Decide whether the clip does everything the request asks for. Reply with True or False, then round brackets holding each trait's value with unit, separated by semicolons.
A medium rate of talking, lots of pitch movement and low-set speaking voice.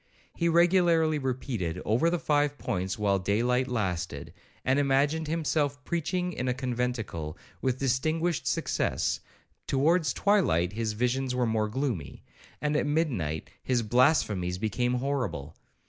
False (130 wpm; 5.9 semitones; 130 Hz)